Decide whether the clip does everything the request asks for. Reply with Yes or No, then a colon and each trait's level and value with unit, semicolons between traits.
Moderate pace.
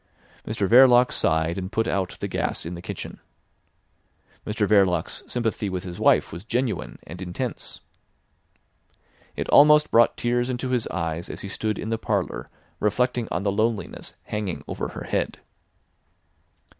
Yes: average, 150 wpm